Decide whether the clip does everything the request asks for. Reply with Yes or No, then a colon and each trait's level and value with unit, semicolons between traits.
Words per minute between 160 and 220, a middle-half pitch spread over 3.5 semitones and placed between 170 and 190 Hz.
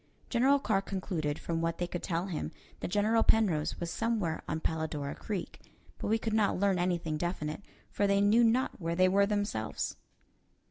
Yes: average, 180 wpm; average, 4.2 semitones; medium, 185 Hz